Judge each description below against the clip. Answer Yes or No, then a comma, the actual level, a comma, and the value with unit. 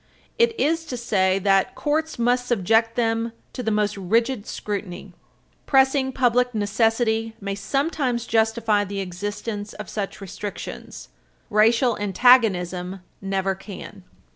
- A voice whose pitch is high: Yes, high, 220 Hz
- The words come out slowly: Yes, slow, 120 wpm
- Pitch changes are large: No, average, 3.7 semitones